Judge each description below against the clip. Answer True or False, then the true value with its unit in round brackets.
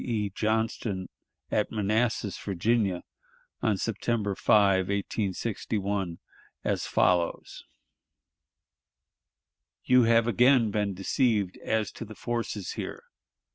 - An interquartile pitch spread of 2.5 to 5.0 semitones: True (2.8 semitones)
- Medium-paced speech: False (95 wpm)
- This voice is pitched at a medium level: False (105 Hz)